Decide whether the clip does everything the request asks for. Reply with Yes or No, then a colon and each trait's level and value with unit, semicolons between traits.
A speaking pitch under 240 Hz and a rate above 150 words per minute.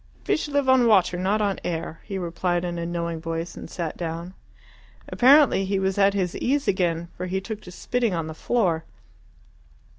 Yes: medium, 185 Hz; average, 185 wpm